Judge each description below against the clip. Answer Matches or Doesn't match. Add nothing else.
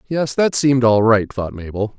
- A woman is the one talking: Doesn't match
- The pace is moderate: Matches